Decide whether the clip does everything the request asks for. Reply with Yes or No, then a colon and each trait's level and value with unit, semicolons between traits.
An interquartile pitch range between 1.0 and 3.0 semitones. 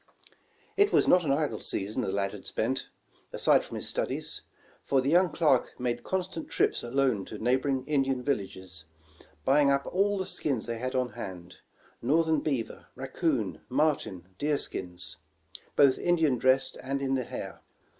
No: average, 4.6 semitones